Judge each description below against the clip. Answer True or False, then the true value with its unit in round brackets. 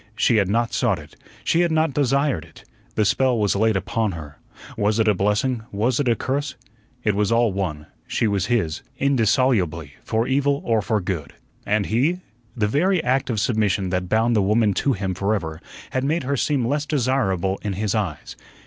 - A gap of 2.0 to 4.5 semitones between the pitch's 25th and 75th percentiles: False (5.1 semitones)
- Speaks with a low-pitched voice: True (110 Hz)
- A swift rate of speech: False (195 wpm)